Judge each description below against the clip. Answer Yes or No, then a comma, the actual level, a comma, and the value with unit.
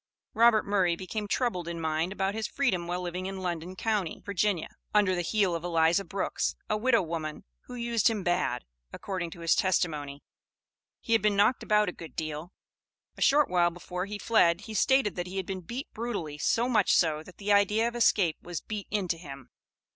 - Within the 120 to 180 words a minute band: No, average, 200 wpm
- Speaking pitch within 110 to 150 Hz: No, medium, 185 Hz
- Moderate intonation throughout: Yes, average, 3.7 semitones